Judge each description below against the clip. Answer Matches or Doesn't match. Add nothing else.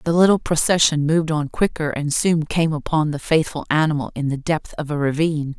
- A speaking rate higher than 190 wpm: Matches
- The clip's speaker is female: Matches